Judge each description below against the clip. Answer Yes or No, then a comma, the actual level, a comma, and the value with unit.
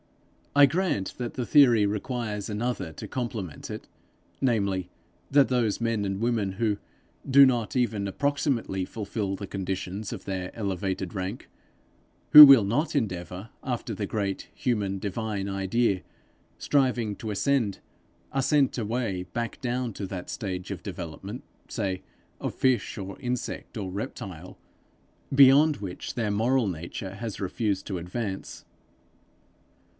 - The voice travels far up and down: No, average, 4.2 semitones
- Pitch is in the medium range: No, low, 105 Hz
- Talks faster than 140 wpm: No, slow, 135 wpm